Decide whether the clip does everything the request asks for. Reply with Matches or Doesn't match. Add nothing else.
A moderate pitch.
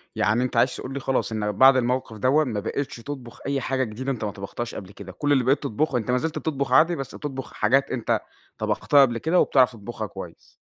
Doesn't match